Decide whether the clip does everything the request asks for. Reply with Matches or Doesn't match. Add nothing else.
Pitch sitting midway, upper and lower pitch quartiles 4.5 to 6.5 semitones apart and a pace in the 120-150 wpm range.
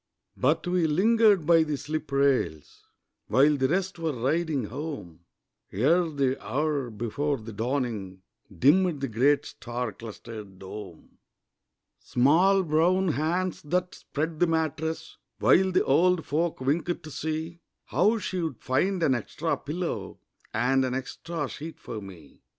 Matches